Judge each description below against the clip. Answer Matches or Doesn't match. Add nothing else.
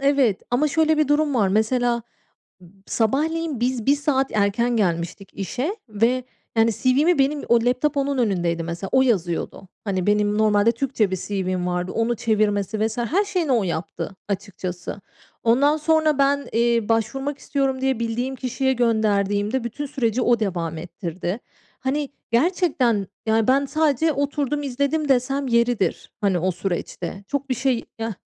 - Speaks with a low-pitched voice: Doesn't match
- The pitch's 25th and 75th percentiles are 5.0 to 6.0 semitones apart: Matches